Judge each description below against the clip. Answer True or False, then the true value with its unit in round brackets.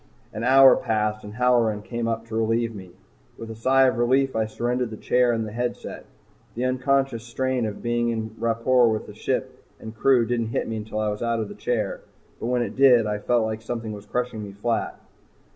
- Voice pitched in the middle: False (115 Hz)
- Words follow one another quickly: True (210 wpm)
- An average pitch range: False (2.1 semitones)